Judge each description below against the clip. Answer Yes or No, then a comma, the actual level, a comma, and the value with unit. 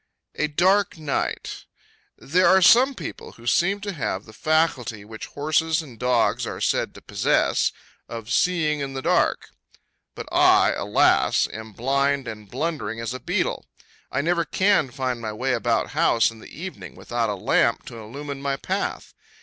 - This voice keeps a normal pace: Yes, average, 165 wpm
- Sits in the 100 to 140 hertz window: Yes, low, 135 Hz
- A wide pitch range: Yes, wide, 5.9 semitones